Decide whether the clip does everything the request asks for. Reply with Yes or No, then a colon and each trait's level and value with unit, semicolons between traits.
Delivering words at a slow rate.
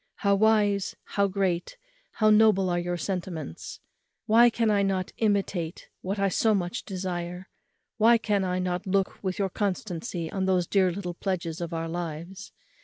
No: average, 165 wpm